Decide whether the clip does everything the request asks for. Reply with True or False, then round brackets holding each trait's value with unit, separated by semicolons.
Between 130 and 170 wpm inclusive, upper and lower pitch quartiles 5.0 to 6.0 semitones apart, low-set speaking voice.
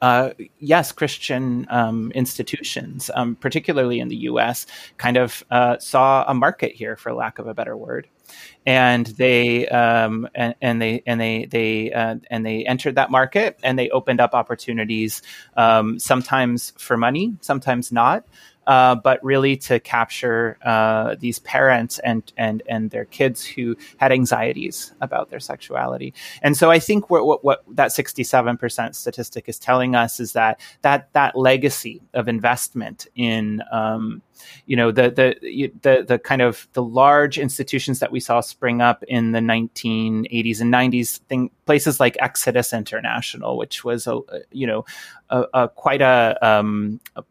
False (165 wpm; 2.5 semitones; 120 Hz)